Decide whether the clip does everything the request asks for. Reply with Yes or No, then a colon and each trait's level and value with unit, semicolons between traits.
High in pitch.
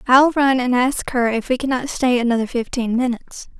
Yes: very high, 250 Hz